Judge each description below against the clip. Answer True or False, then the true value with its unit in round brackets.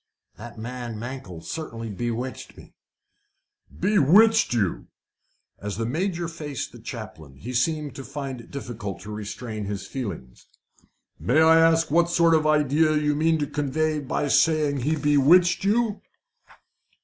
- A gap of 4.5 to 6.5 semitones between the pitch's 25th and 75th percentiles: True (5.6 semitones)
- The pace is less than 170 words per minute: True (140 wpm)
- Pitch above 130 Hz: True (140 Hz)